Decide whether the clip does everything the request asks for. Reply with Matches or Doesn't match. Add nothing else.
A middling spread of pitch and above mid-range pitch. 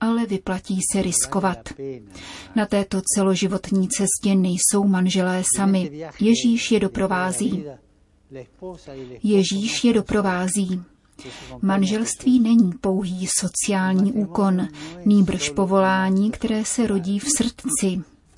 Doesn't match